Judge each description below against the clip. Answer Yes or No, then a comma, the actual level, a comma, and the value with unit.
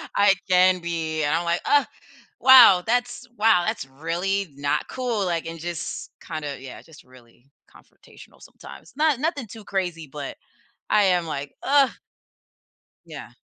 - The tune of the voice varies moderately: No, wide, 5.9 semitones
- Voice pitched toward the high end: No, medium, 175 Hz